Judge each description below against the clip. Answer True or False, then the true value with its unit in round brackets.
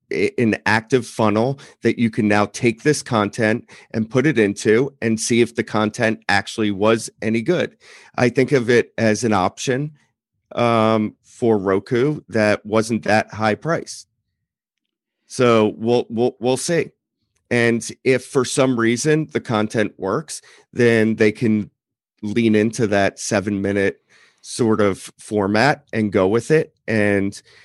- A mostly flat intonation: True (2.3 semitones)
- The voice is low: True (110 Hz)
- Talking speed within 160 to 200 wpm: False (145 wpm)